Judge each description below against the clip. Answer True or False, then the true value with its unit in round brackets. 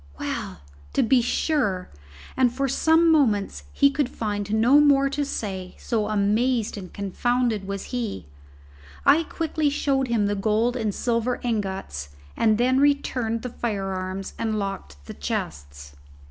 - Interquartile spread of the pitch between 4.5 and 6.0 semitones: True (4.9 semitones)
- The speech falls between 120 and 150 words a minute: True (145 wpm)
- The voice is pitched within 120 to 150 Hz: False (225 Hz)